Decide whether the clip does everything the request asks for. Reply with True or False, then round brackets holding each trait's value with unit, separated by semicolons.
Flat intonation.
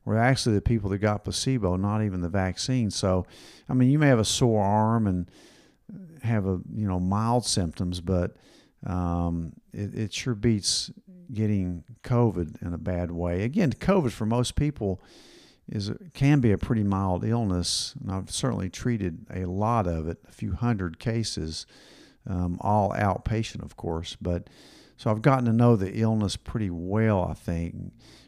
False (4.5 semitones)